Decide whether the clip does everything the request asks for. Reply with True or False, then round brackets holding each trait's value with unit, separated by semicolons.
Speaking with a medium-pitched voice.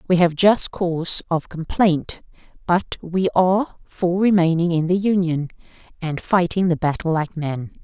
True (175 Hz)